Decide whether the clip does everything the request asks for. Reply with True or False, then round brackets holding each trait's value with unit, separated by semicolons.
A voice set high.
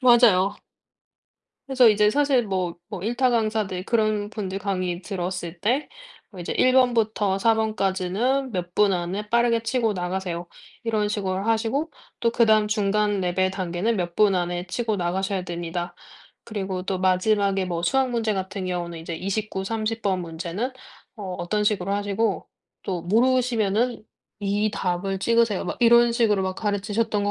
True (205 Hz)